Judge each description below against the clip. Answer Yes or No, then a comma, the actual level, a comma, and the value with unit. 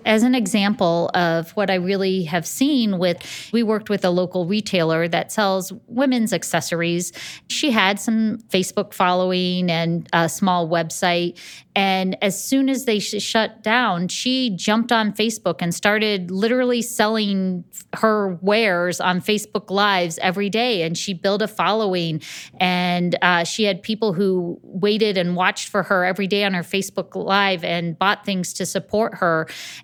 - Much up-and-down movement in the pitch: No, average, 3.2 semitones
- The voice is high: Yes, high, 195 Hz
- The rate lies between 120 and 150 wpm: No, average, 160 wpm